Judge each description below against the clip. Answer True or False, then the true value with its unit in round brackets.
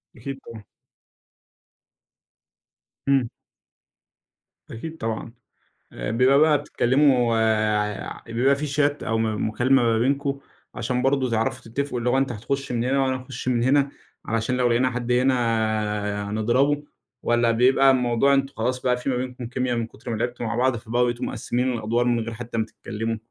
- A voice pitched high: False (125 Hz)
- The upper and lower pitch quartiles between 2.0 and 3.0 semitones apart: True (2.6 semitones)